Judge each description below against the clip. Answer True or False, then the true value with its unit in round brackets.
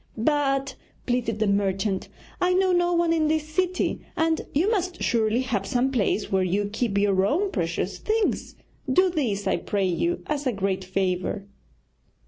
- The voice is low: False (245 Hz)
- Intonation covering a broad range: True (8.7 semitones)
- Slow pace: False (165 wpm)